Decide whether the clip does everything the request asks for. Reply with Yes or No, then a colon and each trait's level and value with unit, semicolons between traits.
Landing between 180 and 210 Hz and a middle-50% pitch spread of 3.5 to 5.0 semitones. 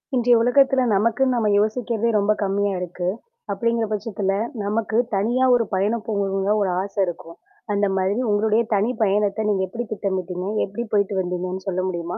No: high, 205 Hz; average, 3.0 semitones